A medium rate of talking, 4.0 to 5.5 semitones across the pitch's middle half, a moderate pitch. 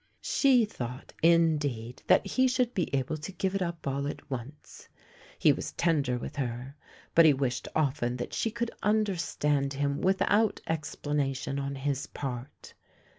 Yes: average, 155 wpm; average, 5.1 semitones; medium, 145 Hz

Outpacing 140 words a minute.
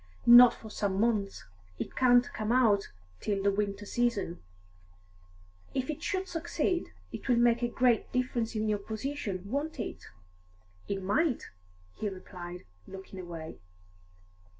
No: slow, 135 wpm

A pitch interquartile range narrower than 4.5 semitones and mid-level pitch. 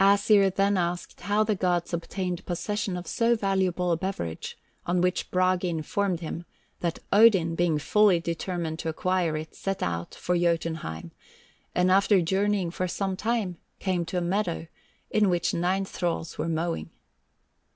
Yes: narrow, 2.5 semitones; medium, 180 Hz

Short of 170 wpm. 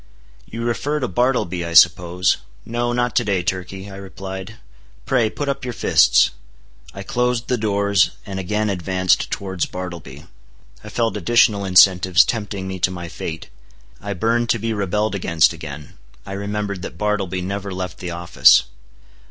Yes: average, 160 wpm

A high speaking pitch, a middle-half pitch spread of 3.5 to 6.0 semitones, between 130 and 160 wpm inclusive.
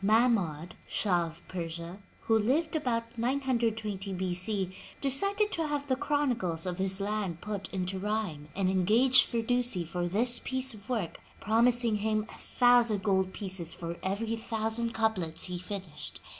Yes: high, 210 Hz; average, 4.4 semitones; average, 150 wpm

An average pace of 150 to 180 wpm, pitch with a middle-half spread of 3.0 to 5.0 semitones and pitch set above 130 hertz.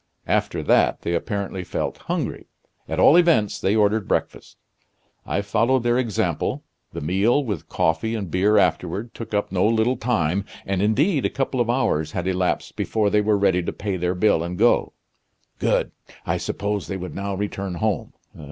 No: average, 175 wpm; average, 3.5 semitones; low, 100 Hz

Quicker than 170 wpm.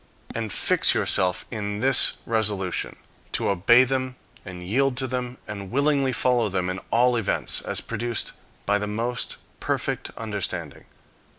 No: average, 140 wpm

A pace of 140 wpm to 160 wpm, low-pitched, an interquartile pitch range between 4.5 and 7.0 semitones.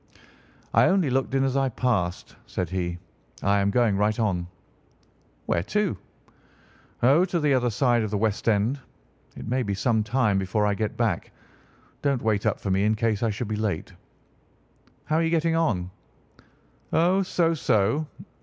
No: average, 175 wpm; low, 110 Hz; average, 5.2 semitones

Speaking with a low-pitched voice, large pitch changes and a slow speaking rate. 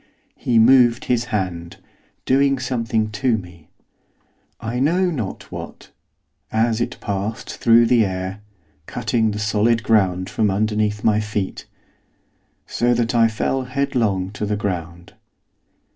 No: low, 110 Hz; average, 2.9 semitones; slow, 130 wpm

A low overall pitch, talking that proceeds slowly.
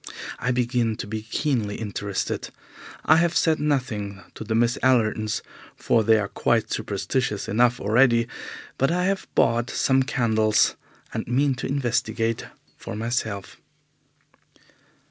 Yes: low, 115 Hz; slow, 130 wpm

